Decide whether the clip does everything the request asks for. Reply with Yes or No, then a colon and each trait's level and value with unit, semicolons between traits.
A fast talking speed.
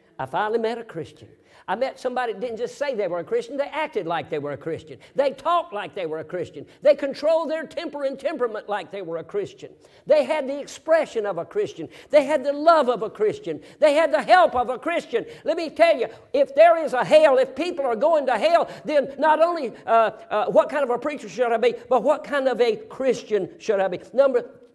Yes: fast, 245 wpm